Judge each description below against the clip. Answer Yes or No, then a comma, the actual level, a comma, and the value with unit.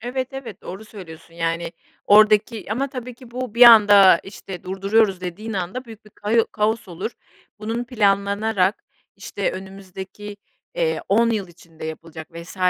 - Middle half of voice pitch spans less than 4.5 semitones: Yes, average, 3.4 semitones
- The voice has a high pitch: Yes, high, 205 Hz